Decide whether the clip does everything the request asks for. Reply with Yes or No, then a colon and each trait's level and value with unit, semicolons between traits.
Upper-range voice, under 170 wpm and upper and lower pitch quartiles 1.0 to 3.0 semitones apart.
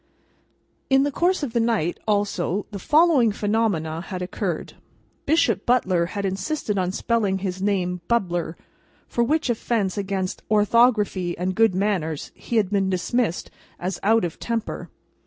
No: high, 205 Hz; average, 145 wpm; average, 4.1 semitones